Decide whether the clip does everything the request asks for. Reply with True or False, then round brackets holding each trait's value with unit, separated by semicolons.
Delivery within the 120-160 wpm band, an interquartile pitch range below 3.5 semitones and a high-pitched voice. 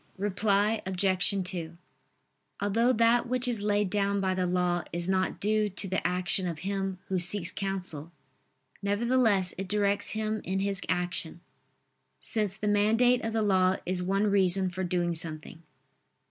True (155 wpm; 2.4 semitones; 195 Hz)